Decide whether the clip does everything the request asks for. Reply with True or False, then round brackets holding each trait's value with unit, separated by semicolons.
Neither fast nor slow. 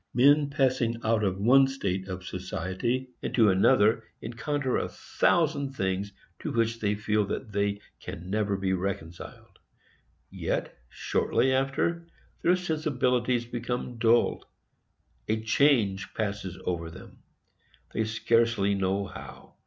False (120 wpm)